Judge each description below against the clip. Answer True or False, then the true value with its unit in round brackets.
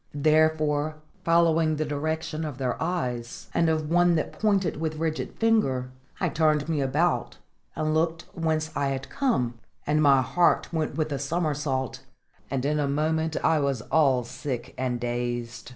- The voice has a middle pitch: True (155 Hz)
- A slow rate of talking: False (160 wpm)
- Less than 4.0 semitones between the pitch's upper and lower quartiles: True (3.1 semitones)